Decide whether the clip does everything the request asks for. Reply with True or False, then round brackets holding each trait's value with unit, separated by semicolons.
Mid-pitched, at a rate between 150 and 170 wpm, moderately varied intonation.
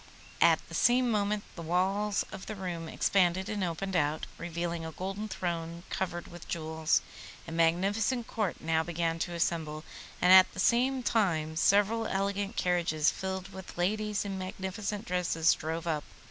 True (180 Hz; 160 wpm; 3.4 semitones)